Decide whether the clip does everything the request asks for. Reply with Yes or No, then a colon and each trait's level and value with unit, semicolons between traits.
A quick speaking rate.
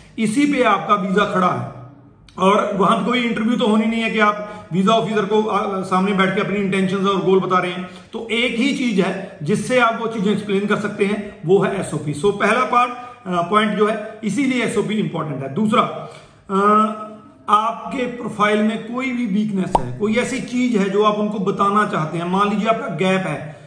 Yes: fast, 200 wpm